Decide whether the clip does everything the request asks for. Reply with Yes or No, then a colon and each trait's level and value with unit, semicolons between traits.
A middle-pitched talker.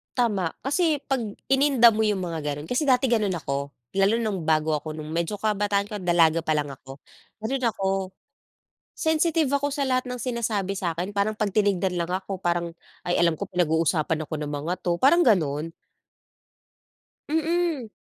No: high, 195 Hz